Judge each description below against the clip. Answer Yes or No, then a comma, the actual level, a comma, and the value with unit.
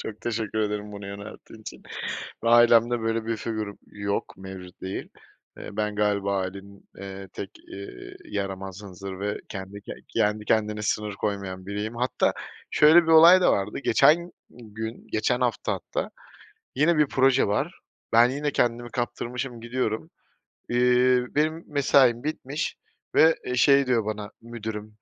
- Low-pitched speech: Yes, low, 110 Hz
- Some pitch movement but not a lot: Yes, average, 3.6 semitones